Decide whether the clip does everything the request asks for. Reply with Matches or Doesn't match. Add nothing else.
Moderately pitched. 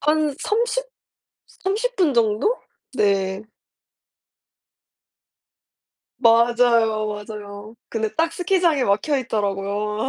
Doesn't match